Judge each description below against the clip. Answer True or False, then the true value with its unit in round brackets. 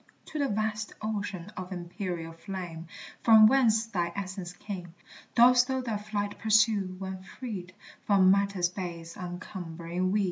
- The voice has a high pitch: True (195 Hz)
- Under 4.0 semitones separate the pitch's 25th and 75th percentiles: True (3.3 semitones)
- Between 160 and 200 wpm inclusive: False (140 wpm)